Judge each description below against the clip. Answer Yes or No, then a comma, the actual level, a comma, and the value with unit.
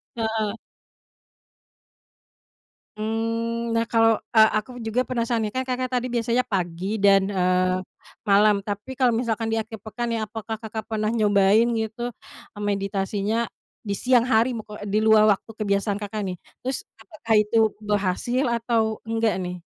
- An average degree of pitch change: No, narrow, 2.2 semitones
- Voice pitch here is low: No, high, 220 Hz